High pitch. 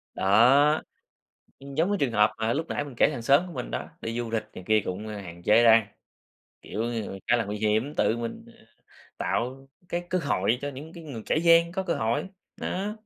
No: low, 120 Hz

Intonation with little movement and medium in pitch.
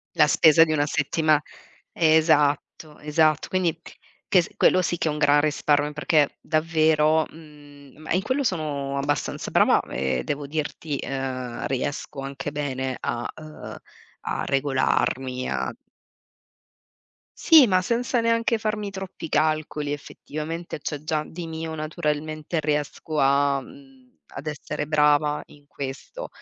Yes: narrow, 2.2 semitones; medium, 150 Hz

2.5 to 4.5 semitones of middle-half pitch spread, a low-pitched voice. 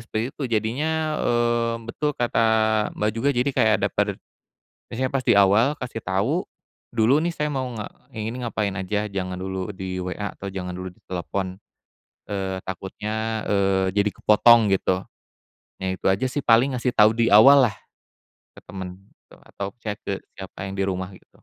Yes: average, 3.9 semitones; low, 105 Hz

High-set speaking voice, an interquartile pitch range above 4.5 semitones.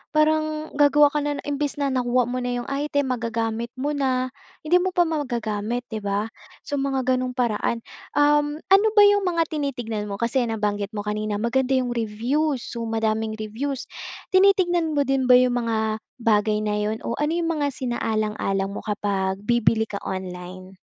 Yes: high, 245 Hz; average, 5.1 semitones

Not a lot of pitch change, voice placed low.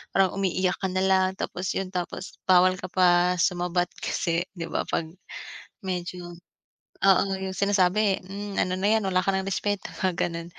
No: narrow, 1.3 semitones; medium, 185 Hz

